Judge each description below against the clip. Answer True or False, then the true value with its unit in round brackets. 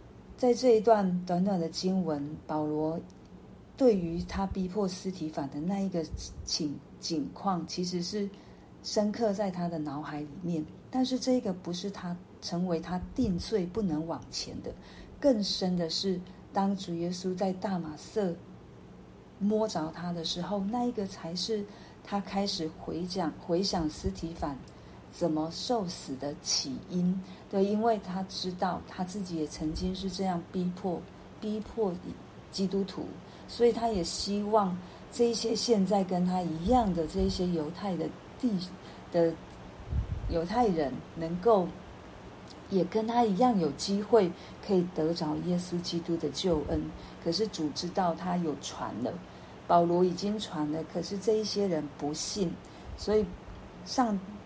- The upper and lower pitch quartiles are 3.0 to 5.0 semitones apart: True (3.6 semitones)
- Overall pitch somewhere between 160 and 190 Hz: True (185 Hz)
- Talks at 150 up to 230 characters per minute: True (210 characters per minute)